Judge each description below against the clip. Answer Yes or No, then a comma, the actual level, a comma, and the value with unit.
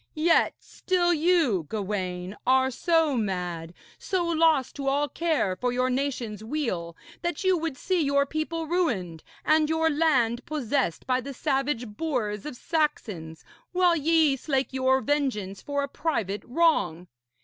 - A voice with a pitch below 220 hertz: No, very high, 275 Hz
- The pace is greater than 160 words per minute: No, average, 145 wpm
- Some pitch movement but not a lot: No, wide, 6.9 semitones